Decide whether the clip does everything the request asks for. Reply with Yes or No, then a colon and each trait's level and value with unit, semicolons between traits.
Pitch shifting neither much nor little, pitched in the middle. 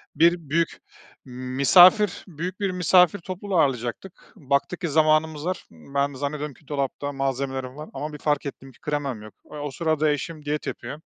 Yes: average, 3.4 semitones; medium, 150 Hz